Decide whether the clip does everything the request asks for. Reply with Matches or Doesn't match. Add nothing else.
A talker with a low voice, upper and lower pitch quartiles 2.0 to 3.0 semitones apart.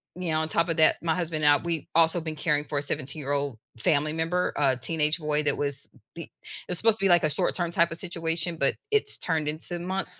Doesn't match